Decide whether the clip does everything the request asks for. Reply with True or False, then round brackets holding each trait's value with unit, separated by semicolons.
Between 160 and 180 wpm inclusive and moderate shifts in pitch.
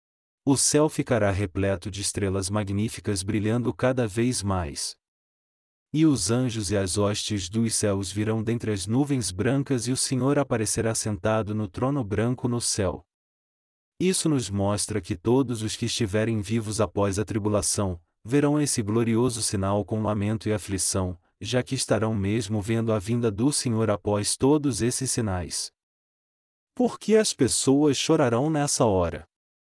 False (150 wpm; 3.6 semitones)